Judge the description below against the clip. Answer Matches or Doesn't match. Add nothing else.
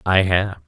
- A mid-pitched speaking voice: Doesn't match